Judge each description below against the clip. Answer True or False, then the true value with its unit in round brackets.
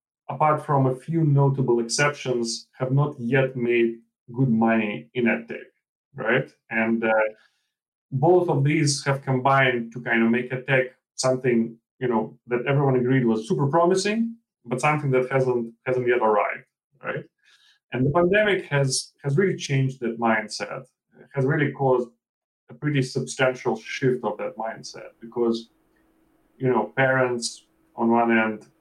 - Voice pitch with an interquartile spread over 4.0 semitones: False (3.1 semitones)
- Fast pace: False (150 wpm)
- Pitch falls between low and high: False (130 Hz)